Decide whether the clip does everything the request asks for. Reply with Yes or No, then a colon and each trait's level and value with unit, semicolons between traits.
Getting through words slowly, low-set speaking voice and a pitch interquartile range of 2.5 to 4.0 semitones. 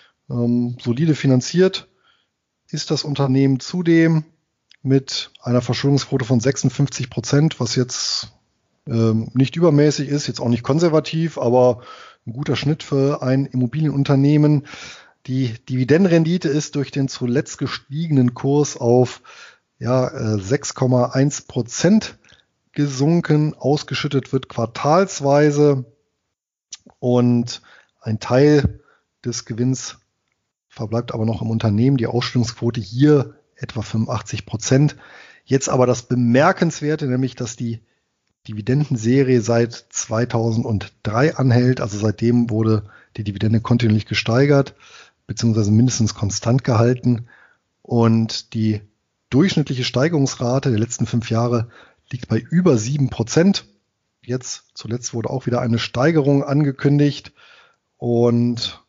Yes: slow, 105 wpm; low, 125 Hz; average, 3.5 semitones